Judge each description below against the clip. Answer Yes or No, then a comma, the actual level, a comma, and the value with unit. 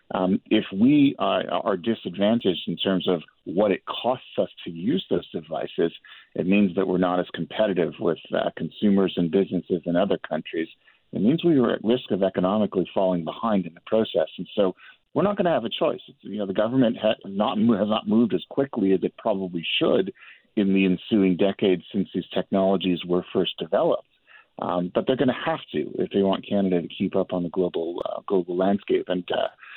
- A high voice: No, very low, 95 Hz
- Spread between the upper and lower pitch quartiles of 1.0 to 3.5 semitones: Yes, average, 2.8 semitones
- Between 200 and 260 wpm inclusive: Yes, fast, 205 wpm